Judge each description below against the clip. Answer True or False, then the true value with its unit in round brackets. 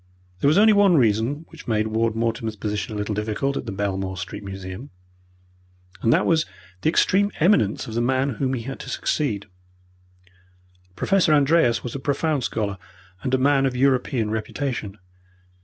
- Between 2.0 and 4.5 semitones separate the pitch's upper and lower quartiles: False (5.0 semitones)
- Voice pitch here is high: False (120 Hz)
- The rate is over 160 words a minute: True (170 wpm)